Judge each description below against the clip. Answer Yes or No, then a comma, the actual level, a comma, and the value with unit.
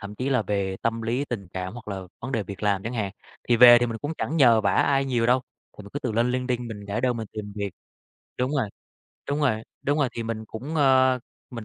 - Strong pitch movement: No, average, 3.6 semitones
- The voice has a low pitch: Yes, low, 115 Hz